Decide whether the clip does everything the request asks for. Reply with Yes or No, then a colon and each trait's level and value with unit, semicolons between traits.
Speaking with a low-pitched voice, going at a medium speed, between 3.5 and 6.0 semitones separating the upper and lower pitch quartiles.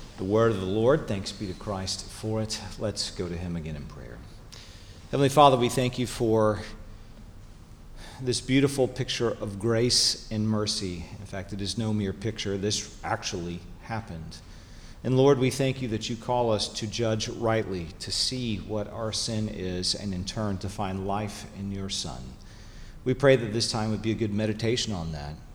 No: low, 105 Hz; average, 190 wpm; average, 3.0 semitones